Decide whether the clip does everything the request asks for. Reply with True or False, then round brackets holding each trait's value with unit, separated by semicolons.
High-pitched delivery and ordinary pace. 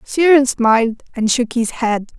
True (240 Hz; 165 wpm)